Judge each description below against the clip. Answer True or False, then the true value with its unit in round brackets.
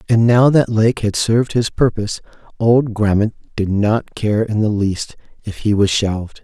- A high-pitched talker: False (110 Hz)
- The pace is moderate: True (185 wpm)